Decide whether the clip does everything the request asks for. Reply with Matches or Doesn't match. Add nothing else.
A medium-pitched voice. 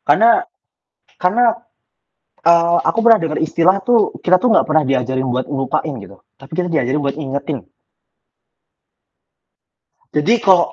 Matches